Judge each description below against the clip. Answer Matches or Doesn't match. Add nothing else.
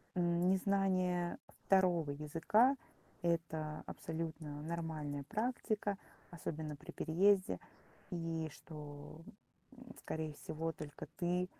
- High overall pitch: Doesn't match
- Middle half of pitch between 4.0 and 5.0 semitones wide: Doesn't match